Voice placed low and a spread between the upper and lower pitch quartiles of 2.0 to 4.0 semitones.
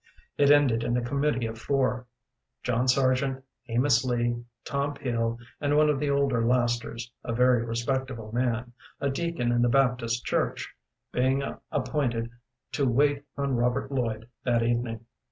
Yes: low, 125 Hz; average, 2.7 semitones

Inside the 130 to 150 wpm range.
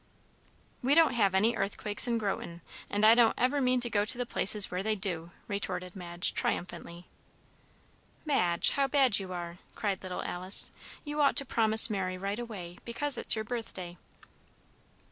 No: average, 165 wpm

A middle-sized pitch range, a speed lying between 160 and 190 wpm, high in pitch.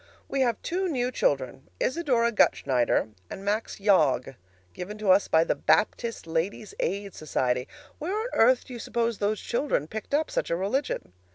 No: wide, 7.3 semitones; average, 170 wpm; high, 210 Hz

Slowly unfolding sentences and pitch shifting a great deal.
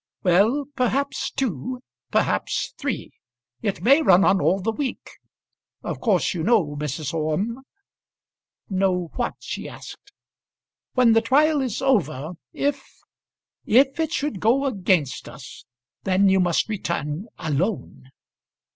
Yes: slow, 130 wpm; wide, 7.2 semitones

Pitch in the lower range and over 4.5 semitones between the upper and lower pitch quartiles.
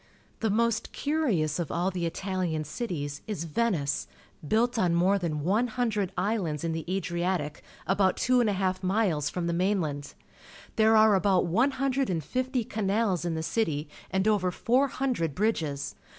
No: high, 190 Hz; average, 5.0 semitones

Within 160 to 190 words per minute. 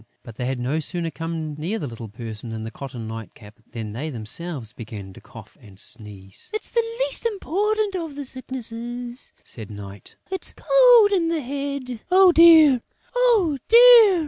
Yes: average, 170 wpm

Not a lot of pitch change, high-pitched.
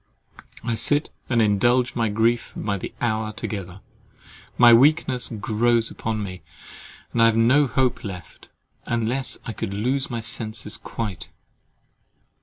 No: narrow, 2.3 semitones; low, 115 Hz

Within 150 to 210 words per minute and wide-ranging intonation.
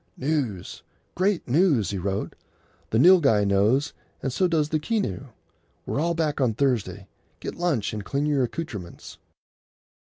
No: average, 140 wpm; wide, 7.4 semitones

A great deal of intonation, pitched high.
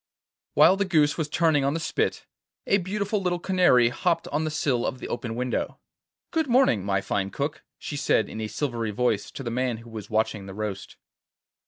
No: wide, 7.2 semitones; low, 135 Hz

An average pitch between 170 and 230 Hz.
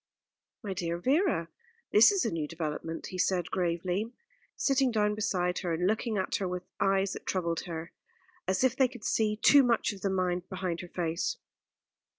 Yes: medium, 185 Hz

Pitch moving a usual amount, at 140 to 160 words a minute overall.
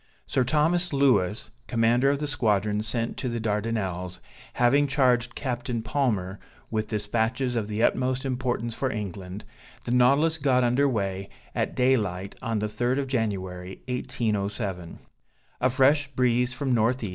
Yes: average, 3.7 semitones; average, 145 wpm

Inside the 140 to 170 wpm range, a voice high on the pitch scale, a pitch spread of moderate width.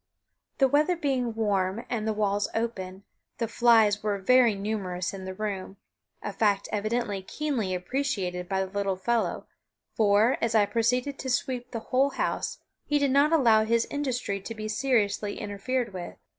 Yes: average, 165 wpm; high, 220 Hz; average, 4.0 semitones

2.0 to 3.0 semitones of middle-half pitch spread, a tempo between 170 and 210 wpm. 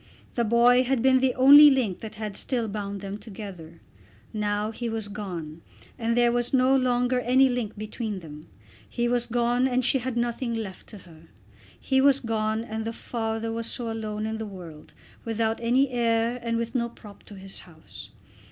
Yes: average, 2.7 semitones; average, 190 wpm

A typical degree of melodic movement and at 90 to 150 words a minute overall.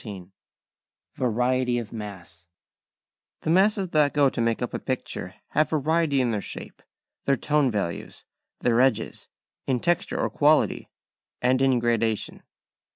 Yes: average, 4.2 semitones; average, 140 wpm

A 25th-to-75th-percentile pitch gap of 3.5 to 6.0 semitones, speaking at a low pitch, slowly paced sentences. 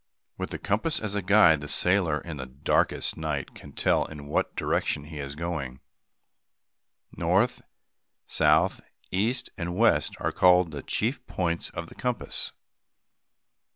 No: average, 4.8 semitones; very low, 85 Hz; average, 145 wpm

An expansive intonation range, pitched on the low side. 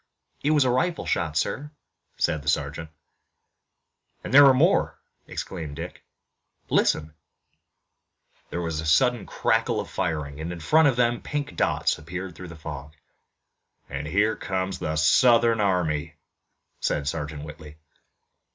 Yes: wide, 7.6 semitones; very low, 85 Hz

